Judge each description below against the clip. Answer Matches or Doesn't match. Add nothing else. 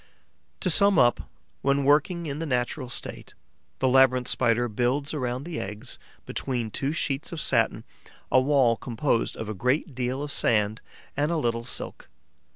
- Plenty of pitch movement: Doesn't match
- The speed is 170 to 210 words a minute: Doesn't match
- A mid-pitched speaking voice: Doesn't match